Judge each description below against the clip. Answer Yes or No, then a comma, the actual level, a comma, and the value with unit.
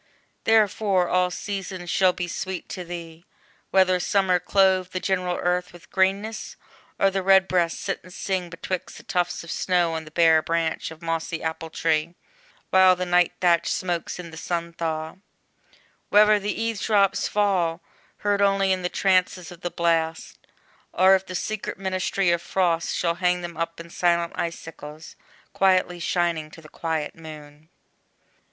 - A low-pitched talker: No, medium, 180 Hz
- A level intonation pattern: Yes, narrow, 2.2 semitones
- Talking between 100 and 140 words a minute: No, average, 160 wpm